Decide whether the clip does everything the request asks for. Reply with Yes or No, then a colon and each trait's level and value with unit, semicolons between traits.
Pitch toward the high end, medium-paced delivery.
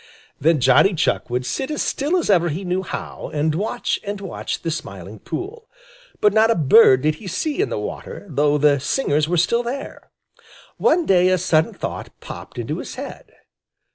No: medium, 180 Hz; average, 190 wpm